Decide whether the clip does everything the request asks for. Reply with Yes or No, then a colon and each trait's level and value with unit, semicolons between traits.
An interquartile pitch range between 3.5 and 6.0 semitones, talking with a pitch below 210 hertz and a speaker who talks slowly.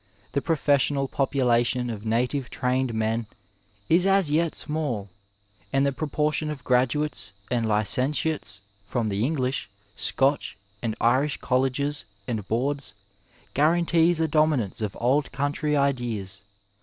Yes: average, 4.2 semitones; low, 135 Hz; slow, 125 wpm